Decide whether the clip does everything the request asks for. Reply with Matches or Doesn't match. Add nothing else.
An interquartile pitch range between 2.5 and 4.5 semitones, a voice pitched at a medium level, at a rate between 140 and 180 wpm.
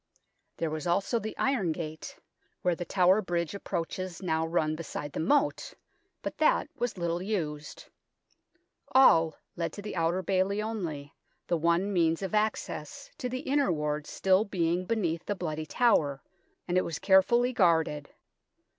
Matches